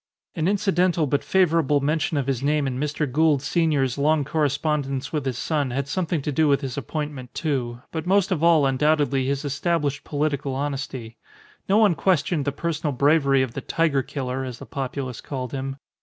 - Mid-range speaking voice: Yes, medium, 145 Hz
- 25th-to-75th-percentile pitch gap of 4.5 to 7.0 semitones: No, average, 2.8 semitones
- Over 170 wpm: Yes, average, 185 wpm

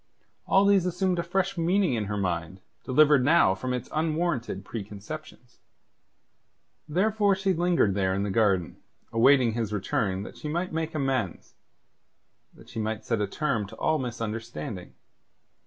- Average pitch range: No, wide, 8.3 semitones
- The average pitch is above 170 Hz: No, low, 125 Hz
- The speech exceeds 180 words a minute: No, average, 150 wpm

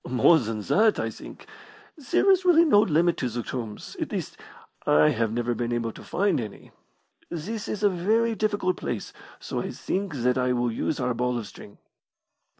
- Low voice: Yes, low, 130 Hz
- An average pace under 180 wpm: No, average, 190 wpm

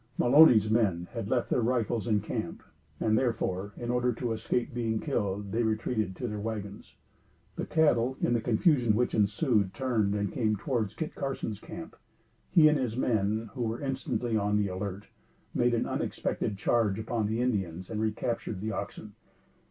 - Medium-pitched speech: No, low, 110 Hz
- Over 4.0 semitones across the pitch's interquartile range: No, average, 2.9 semitones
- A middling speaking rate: Yes, average, 170 wpm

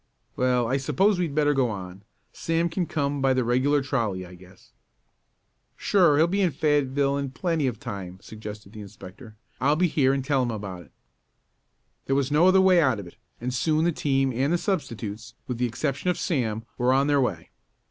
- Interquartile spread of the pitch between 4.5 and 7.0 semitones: Yes, average, 5.0 semitones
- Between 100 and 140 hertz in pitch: Yes, low, 135 Hz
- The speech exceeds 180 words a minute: Yes, average, 200 wpm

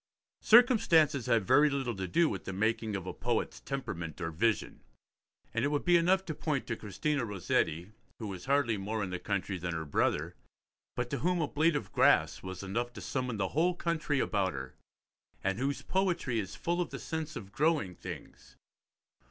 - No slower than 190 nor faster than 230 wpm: Yes, average, 195 wpm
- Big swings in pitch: Yes, wide, 7.9 semitones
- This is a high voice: No, low, 120 Hz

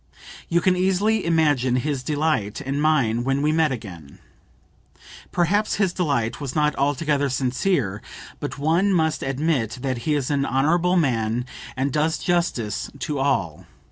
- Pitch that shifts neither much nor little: Yes, average, 4.3 semitones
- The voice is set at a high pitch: No, medium, 145 Hz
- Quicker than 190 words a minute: No, average, 145 wpm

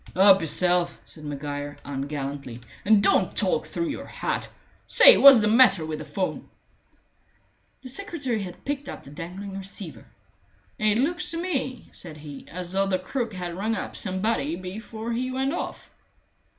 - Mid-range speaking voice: No, high, 195 Hz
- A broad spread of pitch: Yes, wide, 7.2 semitones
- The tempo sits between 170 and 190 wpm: No, average, 160 wpm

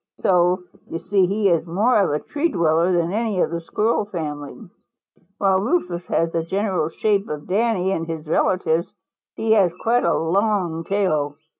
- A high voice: No, medium, 180 Hz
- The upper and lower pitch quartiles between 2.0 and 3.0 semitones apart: No, average, 3.8 semitones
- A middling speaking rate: Yes, average, 170 wpm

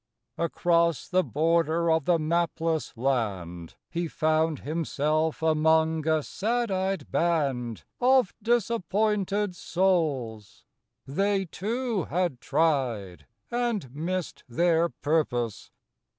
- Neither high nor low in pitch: Yes, medium, 165 Hz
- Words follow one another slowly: Yes, slow, 95 wpm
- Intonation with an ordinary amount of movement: Yes, average, 4.3 semitones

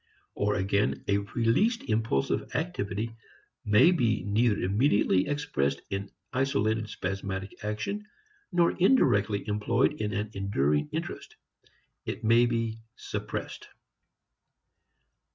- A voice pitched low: Yes, low, 105 Hz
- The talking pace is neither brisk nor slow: No, slow, 100 wpm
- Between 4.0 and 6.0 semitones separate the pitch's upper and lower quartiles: No, average, 3.5 semitones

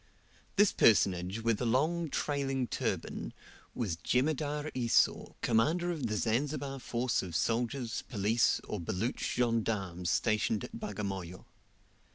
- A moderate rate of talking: No, slow, 120 wpm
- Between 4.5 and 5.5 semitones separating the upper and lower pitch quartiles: Yes, average, 5.1 semitones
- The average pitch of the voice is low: Yes, low, 120 Hz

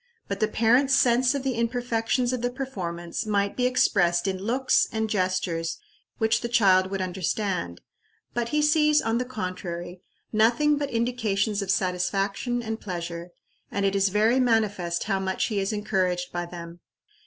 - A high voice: Yes, high, 210 Hz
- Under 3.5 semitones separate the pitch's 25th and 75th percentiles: No, average, 4.7 semitones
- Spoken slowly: No, average, 165 wpm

